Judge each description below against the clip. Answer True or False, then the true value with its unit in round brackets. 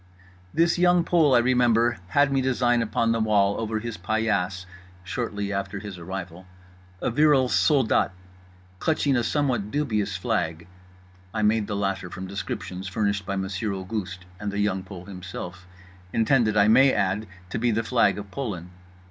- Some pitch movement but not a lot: True (4.4 semitones)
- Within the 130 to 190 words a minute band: True (155 wpm)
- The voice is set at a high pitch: False (105 Hz)